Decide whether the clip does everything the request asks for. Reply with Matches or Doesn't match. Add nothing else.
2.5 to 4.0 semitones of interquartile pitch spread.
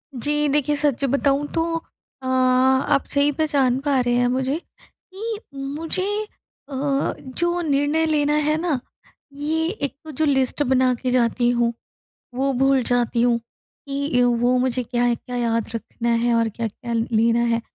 Matches